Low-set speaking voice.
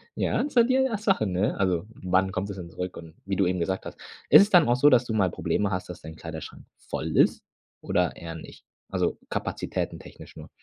Yes: very low, 95 Hz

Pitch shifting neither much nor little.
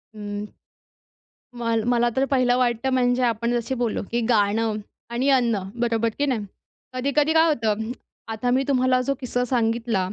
No: narrow, 2.2 semitones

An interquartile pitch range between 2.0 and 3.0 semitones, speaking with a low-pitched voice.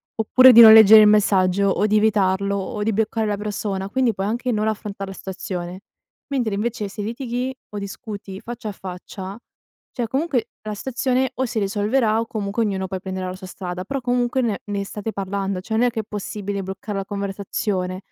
No: narrow, 2.6 semitones; high, 210 Hz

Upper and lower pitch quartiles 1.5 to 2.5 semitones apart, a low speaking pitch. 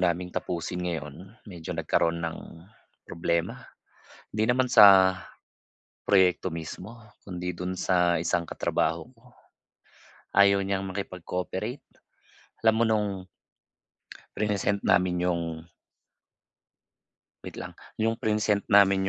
No: average, 2.9 semitones; very low, 95 Hz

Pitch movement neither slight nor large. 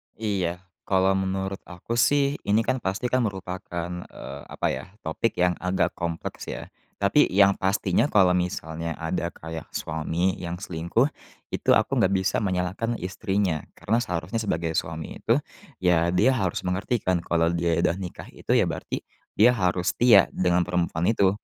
Yes: average, 3.0 semitones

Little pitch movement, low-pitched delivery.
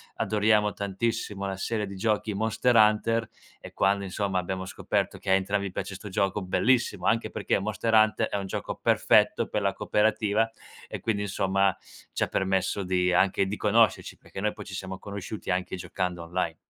Yes: narrow, 2.2 semitones; low, 100 Hz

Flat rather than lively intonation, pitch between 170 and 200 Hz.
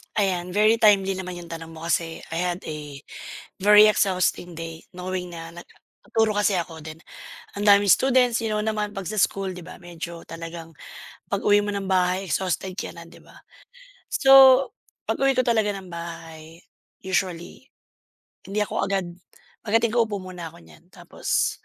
No: average, 3.7 semitones; medium, 185 Hz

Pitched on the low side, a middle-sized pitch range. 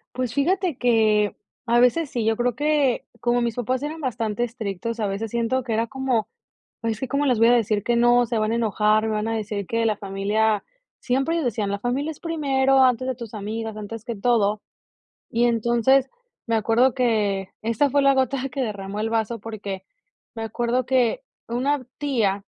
No: high, 235 Hz; average, 3.0 semitones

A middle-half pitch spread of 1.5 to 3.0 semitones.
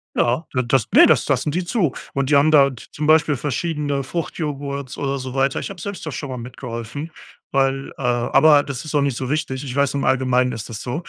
Yes: average, 2.7 semitones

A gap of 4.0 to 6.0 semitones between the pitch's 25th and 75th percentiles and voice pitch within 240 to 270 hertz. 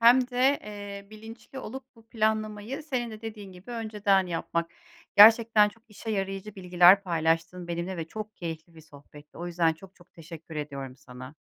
No: average, 4.7 semitones; high, 195 Hz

